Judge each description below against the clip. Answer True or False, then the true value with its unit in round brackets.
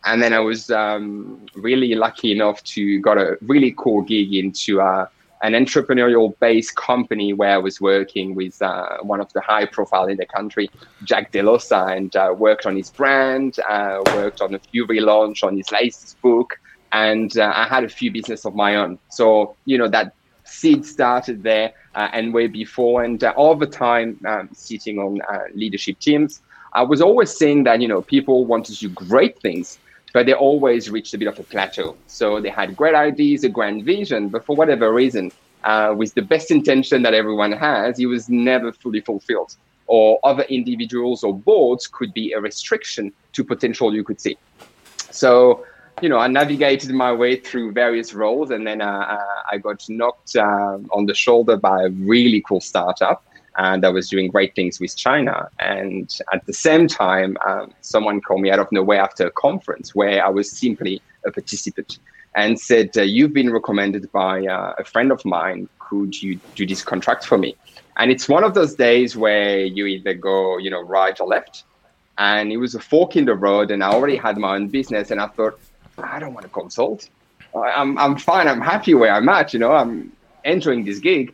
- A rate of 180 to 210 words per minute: True (200 wpm)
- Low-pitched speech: True (110 Hz)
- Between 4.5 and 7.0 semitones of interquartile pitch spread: False (3.7 semitones)